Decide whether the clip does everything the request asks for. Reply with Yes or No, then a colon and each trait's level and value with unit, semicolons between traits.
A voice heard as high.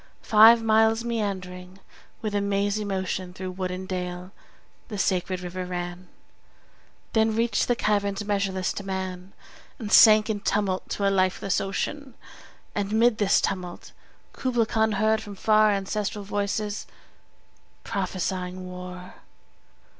Yes: high, 200 Hz